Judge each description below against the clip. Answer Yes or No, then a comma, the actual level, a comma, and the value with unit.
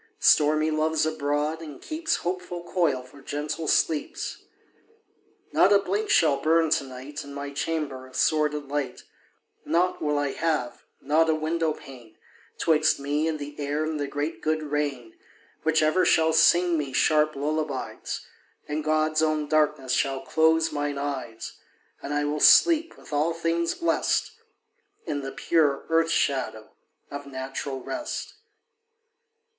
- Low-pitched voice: No, medium, 150 Hz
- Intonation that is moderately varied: No, narrow, 2.2 semitones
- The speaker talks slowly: No, average, 145 wpm